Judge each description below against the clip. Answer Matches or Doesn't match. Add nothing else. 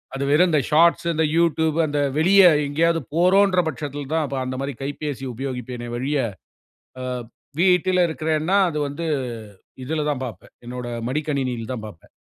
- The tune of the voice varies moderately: Matches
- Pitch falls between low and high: Matches